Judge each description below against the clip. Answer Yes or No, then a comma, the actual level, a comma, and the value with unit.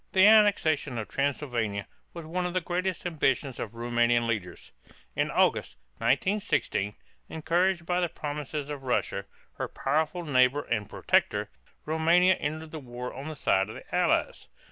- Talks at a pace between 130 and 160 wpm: Yes, average, 150 wpm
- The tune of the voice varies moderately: No, wide, 6.2 semitones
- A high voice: No, medium, 150 Hz